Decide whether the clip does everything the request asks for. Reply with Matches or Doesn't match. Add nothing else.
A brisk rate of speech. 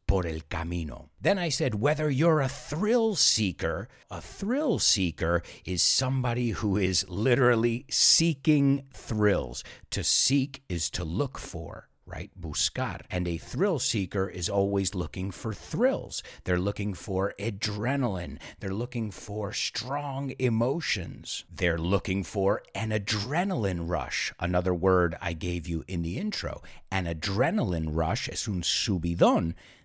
Doesn't match